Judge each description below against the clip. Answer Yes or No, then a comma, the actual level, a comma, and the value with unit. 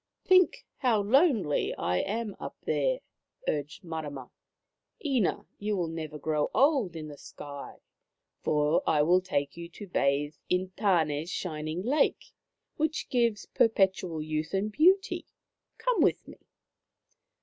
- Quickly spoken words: No, slow, 135 wpm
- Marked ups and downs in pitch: Yes, wide, 7.2 semitones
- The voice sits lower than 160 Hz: No, medium, 180 Hz